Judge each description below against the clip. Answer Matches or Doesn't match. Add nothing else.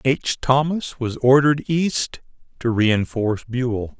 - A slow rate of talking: Matches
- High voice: Doesn't match